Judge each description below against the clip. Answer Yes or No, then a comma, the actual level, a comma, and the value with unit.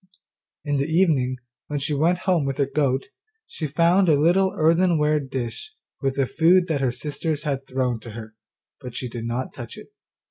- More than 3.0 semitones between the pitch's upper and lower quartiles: Yes, average, 4.0 semitones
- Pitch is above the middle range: No, medium, 145 Hz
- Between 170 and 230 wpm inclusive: Yes, average, 185 wpm